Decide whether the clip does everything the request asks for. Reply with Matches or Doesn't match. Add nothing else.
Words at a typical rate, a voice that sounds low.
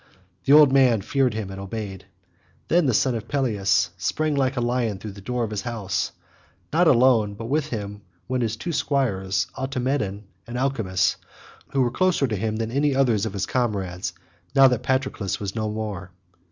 Matches